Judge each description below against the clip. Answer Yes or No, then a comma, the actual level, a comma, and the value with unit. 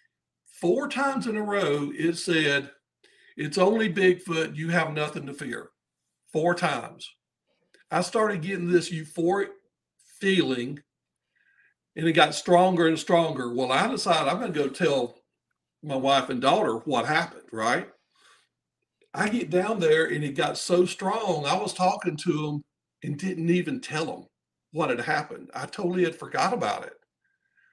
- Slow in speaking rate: No, average, 155 wpm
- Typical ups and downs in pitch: Yes, average, 4.2 semitones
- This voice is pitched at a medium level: Yes, medium, 170 Hz